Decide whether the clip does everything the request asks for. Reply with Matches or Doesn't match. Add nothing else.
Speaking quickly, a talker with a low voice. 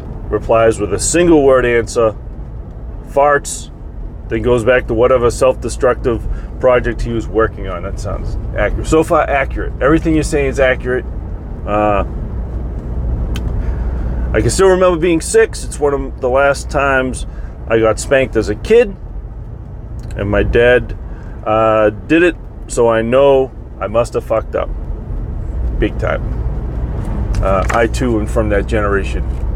Doesn't match